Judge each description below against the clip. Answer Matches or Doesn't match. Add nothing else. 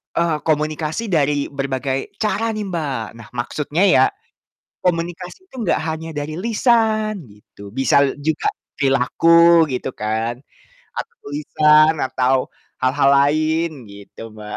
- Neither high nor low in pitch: Matches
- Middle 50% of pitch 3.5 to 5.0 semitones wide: Matches